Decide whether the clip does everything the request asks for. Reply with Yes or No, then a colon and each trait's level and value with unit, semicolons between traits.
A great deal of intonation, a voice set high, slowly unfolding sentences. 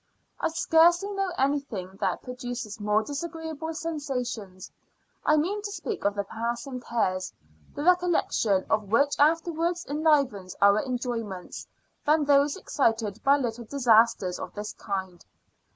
Yes: wide, 6.8 semitones; very high, 250 Hz; slow, 130 wpm